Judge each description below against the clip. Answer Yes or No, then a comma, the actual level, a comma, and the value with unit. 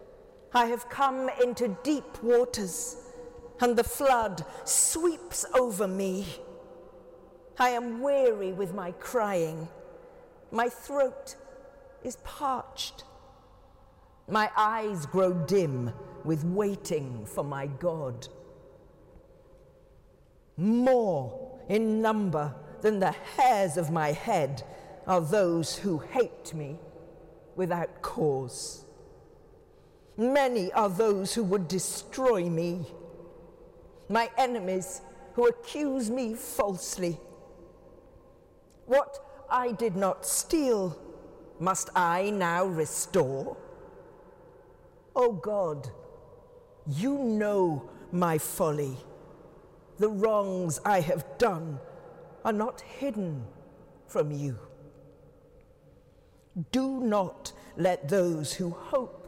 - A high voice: Yes, high, 210 Hz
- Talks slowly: Yes, slow, 95 wpm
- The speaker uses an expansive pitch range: Yes, wide, 6.8 semitones